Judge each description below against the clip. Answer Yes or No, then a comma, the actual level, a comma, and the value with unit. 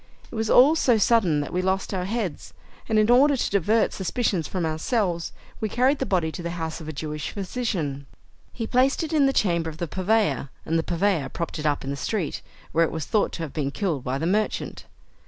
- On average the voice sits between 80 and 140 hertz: No, medium, 185 Hz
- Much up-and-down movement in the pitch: Yes, wide, 5.8 semitones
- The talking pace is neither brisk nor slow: No, fast, 230 wpm